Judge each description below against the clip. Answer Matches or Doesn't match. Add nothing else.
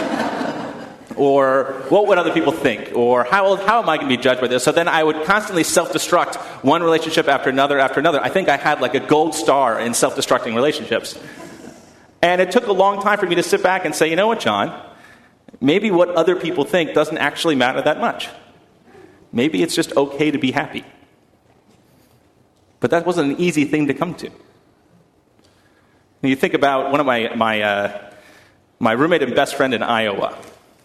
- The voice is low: Doesn't match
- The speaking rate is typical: Matches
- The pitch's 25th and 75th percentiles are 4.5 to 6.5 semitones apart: Matches